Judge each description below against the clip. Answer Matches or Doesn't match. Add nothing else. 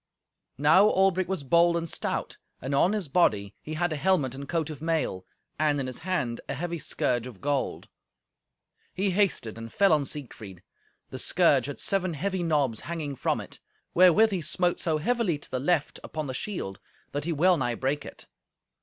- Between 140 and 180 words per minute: Doesn't match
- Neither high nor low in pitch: Matches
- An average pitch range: Matches